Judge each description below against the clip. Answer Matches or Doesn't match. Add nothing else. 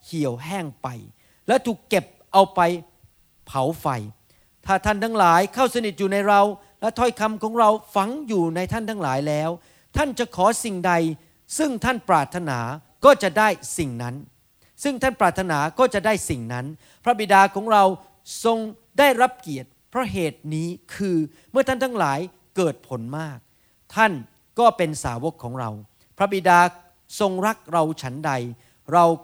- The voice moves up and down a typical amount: Doesn't match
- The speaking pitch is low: Doesn't match